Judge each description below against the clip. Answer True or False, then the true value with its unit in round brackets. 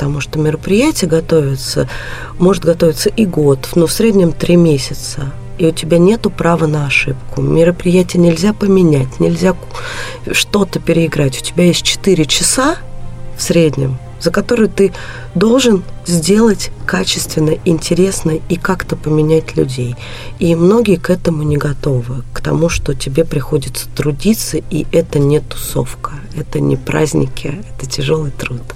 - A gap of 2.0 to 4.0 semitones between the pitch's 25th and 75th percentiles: False (4.7 semitones)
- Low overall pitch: False (160 Hz)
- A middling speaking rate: True (140 wpm)